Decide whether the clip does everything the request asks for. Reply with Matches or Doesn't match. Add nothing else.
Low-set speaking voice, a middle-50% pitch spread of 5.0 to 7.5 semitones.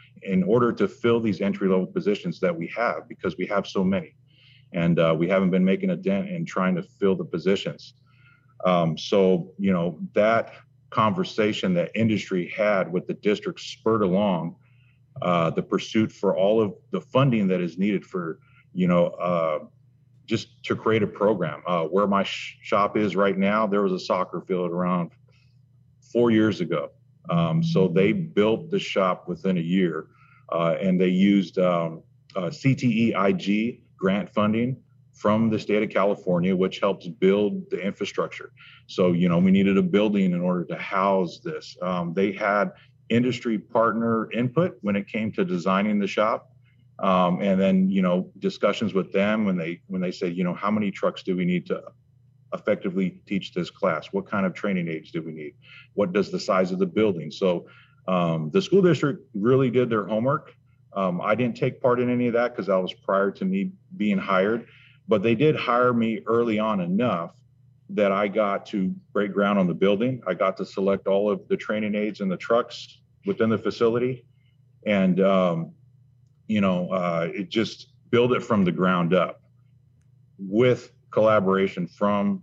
Matches